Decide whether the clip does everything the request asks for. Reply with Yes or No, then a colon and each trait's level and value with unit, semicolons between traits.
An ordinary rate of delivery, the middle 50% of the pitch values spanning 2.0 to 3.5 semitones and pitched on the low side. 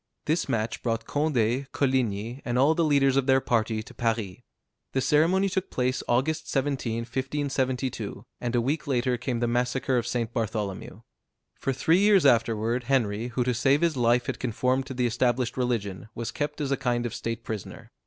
Yes: average, 185 wpm; average, 2.8 semitones; low, 125 Hz